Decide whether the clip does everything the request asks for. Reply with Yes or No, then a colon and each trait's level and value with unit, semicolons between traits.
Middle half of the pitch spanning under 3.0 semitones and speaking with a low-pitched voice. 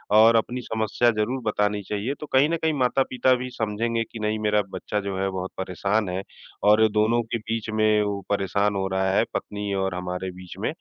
Yes: narrow, 2.6 semitones; low, 105 Hz